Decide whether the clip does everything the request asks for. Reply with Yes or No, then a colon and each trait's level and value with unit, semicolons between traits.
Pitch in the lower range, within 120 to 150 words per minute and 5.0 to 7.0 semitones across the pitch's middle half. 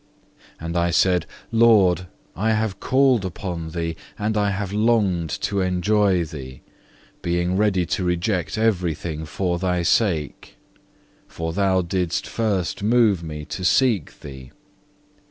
No: very low, 90 Hz; slow, 135 wpm; average, 3.7 semitones